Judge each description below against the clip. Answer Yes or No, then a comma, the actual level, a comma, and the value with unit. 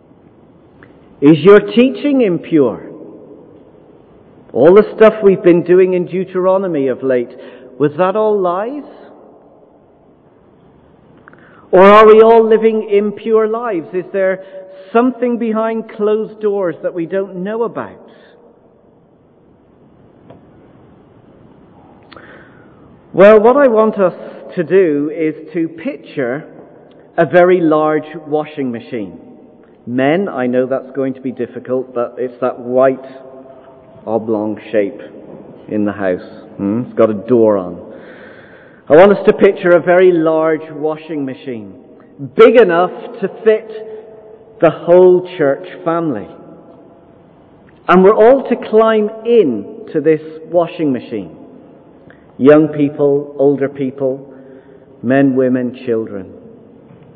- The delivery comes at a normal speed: No, slow, 115 wpm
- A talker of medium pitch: Yes, medium, 170 Hz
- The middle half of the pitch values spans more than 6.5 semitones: Yes, wide, 7.8 semitones